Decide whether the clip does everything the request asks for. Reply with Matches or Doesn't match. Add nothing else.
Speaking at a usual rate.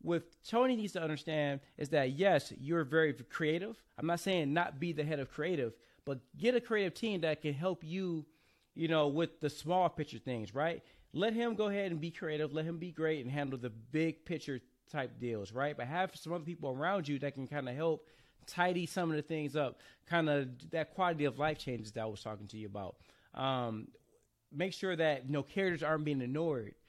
Doesn't match